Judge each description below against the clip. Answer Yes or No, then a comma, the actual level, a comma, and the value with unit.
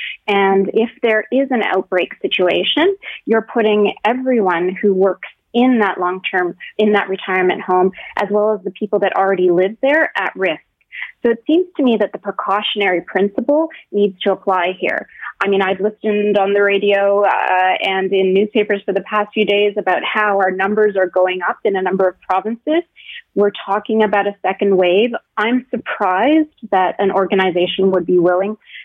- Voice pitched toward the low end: No, high, 200 Hz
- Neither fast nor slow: Yes, average, 180 wpm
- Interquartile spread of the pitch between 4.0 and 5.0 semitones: No, narrow, 2.6 semitones